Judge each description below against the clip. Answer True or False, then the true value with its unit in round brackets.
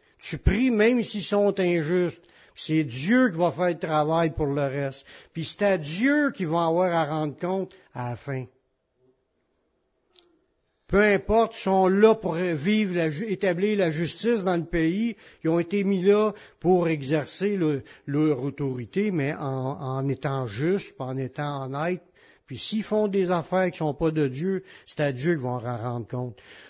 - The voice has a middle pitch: True (170 Hz)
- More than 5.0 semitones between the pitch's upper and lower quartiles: True (5.5 semitones)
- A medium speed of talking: True (180 wpm)